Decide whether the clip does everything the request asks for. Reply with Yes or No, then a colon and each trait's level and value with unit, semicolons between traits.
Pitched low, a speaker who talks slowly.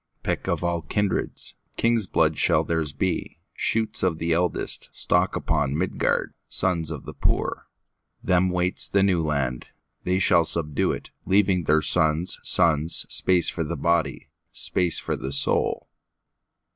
Yes: very low, 85 Hz; slow, 115 wpm